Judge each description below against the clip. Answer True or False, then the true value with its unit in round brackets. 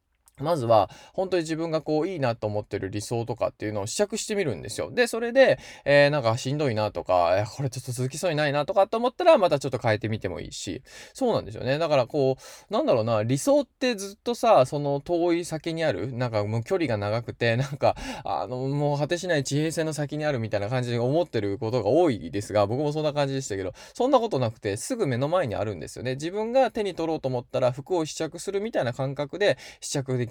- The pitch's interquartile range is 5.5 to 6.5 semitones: True (6.2 semitones)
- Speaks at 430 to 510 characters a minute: True (475 characters per minute)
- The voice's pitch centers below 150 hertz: True (140 Hz)